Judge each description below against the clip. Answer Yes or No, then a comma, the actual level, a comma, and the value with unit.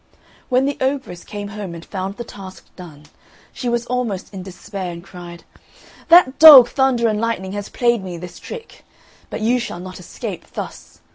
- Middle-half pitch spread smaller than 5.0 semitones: No, average, 5.3 semitones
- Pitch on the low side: No, high, 205 Hz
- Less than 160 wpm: No, average, 180 wpm